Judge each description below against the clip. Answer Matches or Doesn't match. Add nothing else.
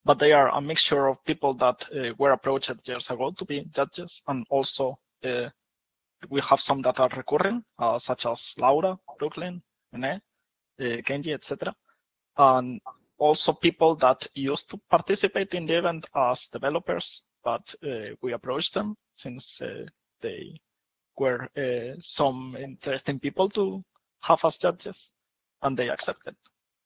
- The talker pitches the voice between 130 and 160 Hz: Matches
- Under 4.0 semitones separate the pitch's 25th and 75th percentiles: Doesn't match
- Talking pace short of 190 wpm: Matches